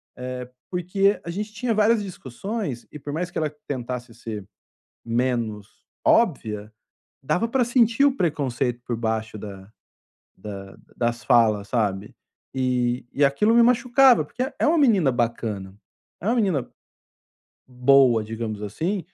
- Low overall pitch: Yes, low, 130 Hz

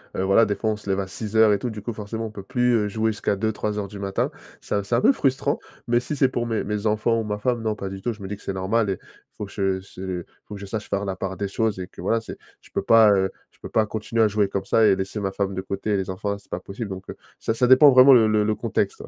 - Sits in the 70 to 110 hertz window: Yes, low, 105 Hz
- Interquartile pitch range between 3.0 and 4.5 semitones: No, narrow, 2.4 semitones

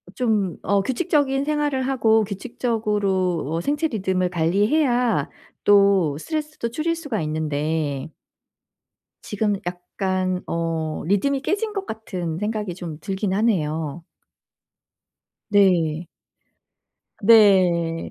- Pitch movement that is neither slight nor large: No, wide, 5.9 semitones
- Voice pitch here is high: Yes, high, 200 Hz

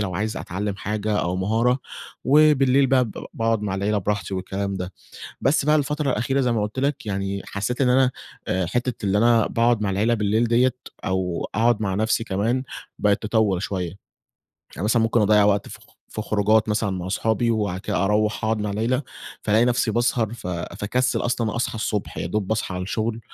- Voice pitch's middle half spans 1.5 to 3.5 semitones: Yes, average, 3.1 semitones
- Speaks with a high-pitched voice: No, low, 110 Hz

